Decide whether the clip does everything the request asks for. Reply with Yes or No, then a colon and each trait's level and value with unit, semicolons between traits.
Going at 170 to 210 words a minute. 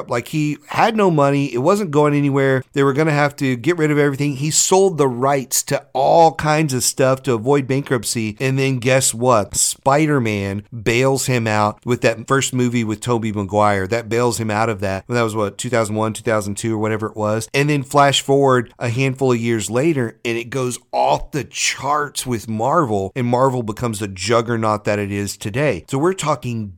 Yes: fast, 205 wpm